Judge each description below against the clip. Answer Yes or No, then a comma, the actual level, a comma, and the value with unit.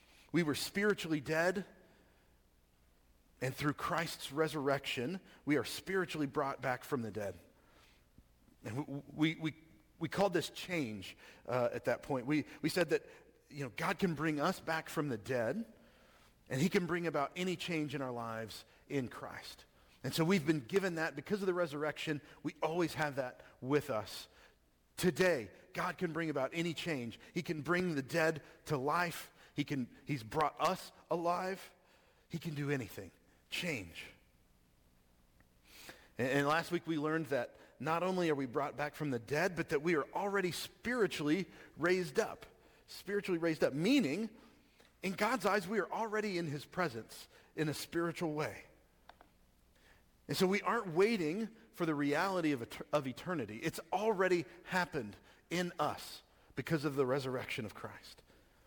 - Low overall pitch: No, medium, 155 Hz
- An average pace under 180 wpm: Yes, average, 165 wpm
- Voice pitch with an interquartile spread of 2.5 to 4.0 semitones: No, average, 5.3 semitones